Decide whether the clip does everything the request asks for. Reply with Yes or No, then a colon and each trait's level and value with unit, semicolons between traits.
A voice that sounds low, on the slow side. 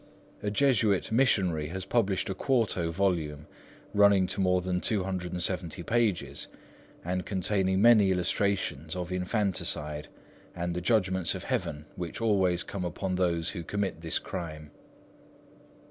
Yes: very low, 95 Hz; slow, 130 wpm